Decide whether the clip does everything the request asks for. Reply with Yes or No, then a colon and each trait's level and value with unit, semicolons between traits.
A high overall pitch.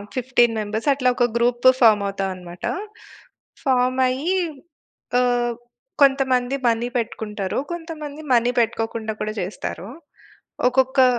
Yes: high, 245 Hz